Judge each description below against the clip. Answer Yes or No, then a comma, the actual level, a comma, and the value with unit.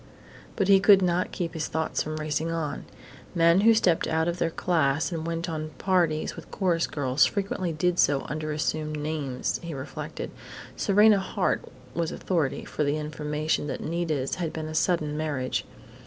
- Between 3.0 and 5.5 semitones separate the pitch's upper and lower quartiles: No, narrow, 2.6 semitones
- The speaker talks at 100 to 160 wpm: No, average, 170 wpm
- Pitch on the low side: No, medium, 160 Hz